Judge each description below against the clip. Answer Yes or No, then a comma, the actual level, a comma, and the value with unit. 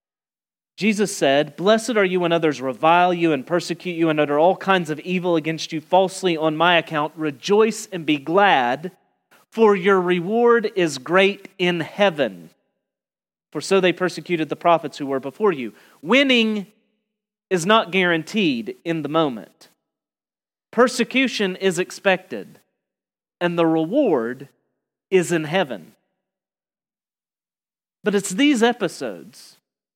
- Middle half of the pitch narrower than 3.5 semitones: No, average, 4.0 semitones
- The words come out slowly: Yes, slow, 130 wpm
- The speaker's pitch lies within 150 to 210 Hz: Yes, medium, 185 Hz